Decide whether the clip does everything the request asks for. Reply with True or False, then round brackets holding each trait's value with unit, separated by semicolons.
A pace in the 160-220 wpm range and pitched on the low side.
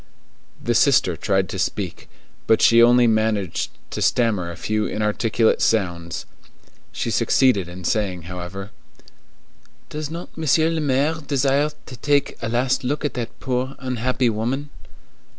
False (140 wpm; 115 Hz)